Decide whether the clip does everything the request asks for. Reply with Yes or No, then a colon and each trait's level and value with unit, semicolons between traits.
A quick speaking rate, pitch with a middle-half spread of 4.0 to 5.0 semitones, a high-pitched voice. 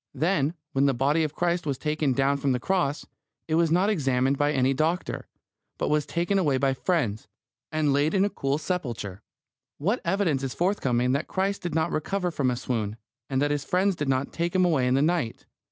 No: fast, 210 wpm; average, 4.5 semitones; medium, 150 Hz